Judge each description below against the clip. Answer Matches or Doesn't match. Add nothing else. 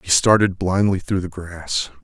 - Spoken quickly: Doesn't match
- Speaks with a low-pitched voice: Matches